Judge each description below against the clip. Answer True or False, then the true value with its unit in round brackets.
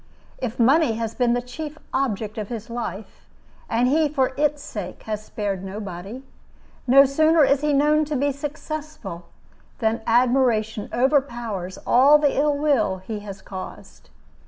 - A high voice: True (245 Hz)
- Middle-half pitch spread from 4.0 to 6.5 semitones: True (5.1 semitones)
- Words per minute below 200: True (150 wpm)